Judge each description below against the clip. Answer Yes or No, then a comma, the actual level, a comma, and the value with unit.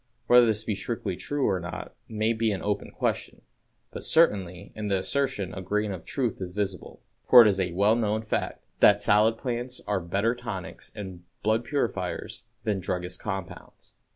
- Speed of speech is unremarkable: Yes, average, 180 wpm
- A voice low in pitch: Yes, low, 105 Hz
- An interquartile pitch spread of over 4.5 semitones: No, average, 3.3 semitones